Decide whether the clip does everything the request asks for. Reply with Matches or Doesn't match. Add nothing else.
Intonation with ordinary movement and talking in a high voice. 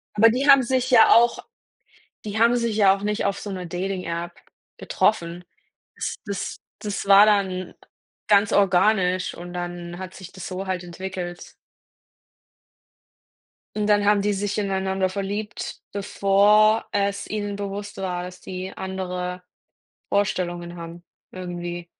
Doesn't match